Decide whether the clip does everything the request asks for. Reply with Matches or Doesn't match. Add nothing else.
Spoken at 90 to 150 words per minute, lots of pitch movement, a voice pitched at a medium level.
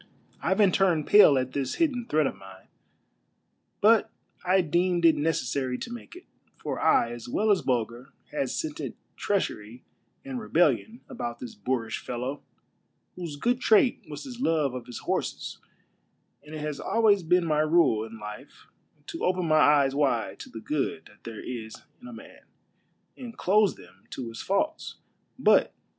Doesn't match